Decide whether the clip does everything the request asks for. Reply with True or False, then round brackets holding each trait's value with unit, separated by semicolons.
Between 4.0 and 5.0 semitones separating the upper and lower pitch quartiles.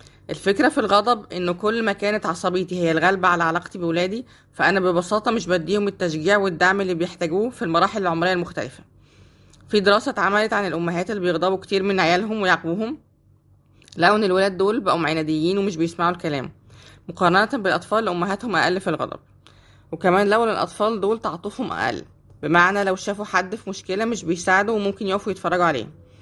False (3.1 semitones)